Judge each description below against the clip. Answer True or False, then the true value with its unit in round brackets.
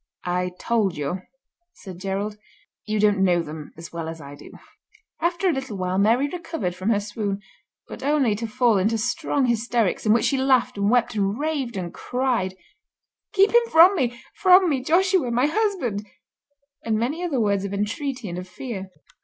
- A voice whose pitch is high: True (225 Hz)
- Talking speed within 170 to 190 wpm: True (180 wpm)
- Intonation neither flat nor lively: False (5.8 semitones)